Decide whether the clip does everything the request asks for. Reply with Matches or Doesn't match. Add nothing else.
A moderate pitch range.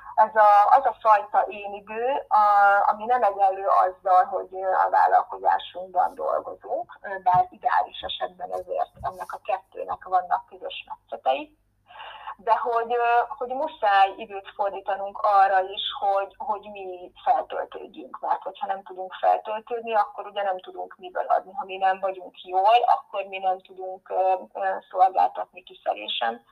Matches